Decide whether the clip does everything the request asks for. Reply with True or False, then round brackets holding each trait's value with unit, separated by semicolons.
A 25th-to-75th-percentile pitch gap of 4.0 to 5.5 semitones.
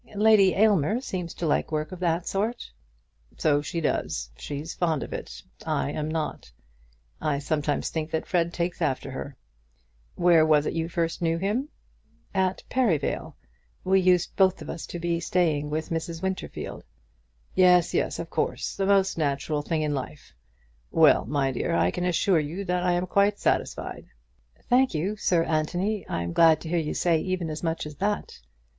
False (3.4 semitones)